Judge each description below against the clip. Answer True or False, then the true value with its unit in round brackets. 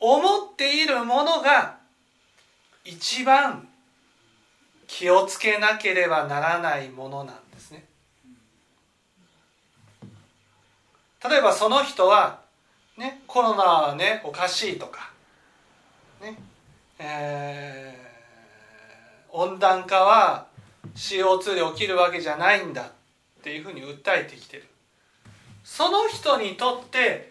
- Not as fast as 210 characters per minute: True (195 characters per minute)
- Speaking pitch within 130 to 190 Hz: True (185 Hz)